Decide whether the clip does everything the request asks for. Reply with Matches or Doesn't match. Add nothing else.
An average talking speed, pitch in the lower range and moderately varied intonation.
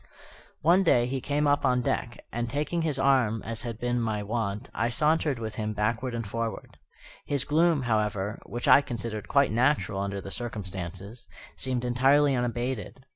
Matches